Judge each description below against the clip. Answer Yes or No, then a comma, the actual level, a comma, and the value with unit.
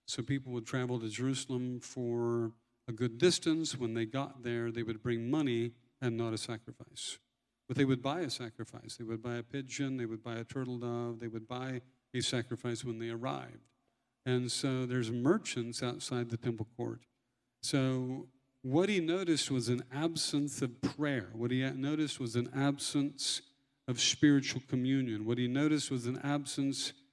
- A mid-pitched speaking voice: No, low, 125 Hz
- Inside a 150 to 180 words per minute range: Yes, average, 175 wpm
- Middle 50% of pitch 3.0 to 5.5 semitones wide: No, narrow, 2.5 semitones